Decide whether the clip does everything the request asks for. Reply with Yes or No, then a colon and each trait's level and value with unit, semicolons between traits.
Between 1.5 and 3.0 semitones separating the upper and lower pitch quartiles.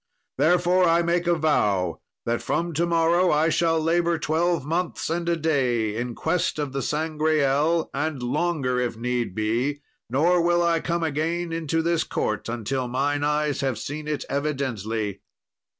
No: average, 4.6 semitones